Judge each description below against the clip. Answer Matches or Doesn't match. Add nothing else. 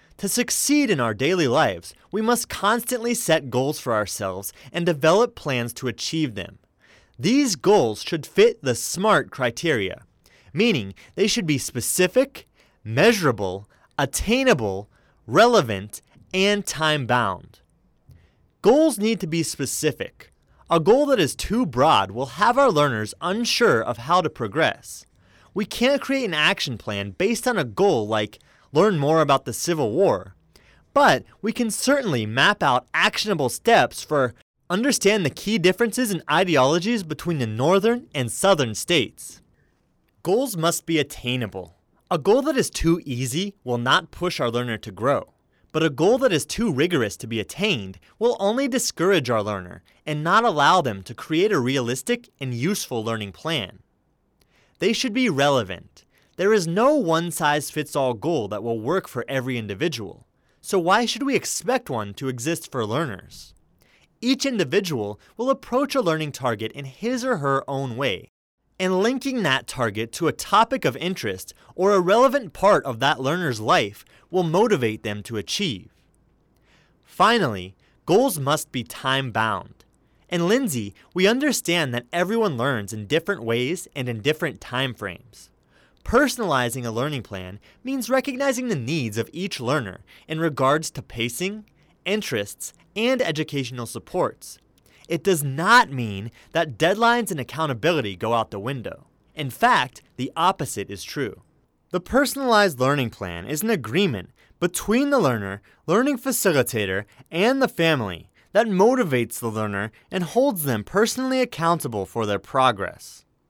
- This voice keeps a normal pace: Matches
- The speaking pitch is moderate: Matches